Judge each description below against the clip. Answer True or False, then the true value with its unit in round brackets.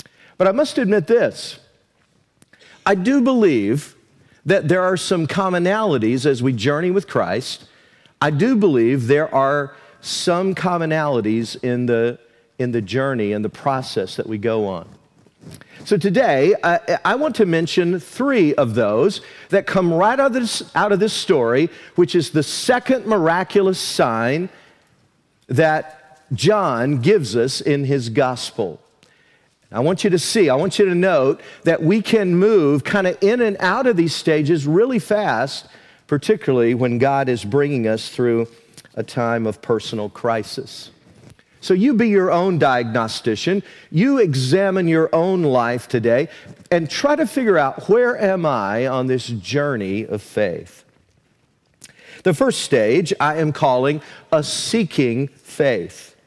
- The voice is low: False (155 Hz)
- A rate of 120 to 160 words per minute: True (150 wpm)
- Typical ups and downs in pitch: False (7.1 semitones)